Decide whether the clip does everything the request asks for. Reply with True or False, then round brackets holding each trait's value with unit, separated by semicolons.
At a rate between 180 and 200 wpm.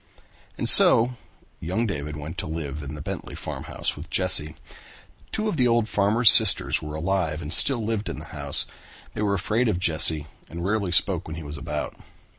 True (190 wpm)